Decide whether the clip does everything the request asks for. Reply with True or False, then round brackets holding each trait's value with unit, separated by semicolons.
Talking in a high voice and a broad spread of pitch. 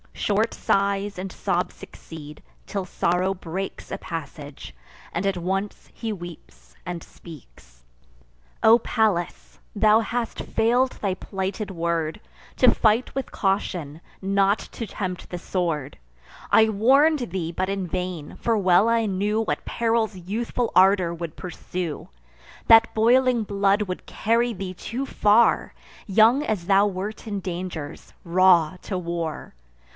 False (195 Hz; 4.0 semitones)